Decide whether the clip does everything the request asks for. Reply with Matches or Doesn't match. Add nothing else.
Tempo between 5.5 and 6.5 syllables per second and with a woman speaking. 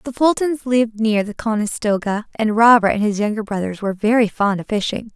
Matches